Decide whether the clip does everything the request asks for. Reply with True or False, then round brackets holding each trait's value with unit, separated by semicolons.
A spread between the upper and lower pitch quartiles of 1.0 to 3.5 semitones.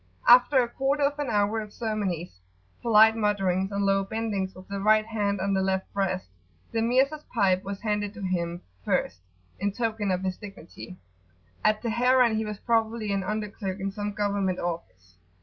True (2.8 semitones)